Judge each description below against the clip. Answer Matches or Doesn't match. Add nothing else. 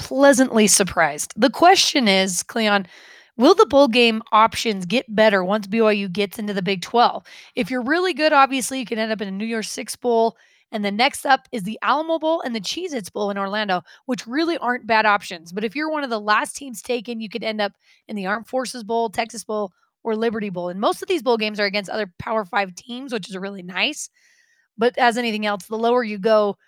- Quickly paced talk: Matches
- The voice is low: Doesn't match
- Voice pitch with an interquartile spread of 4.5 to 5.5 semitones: Doesn't match